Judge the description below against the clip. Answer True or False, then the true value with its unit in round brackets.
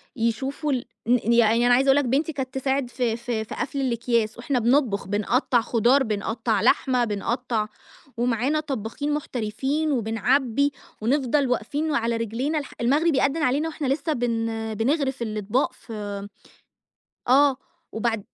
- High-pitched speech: True (245 Hz)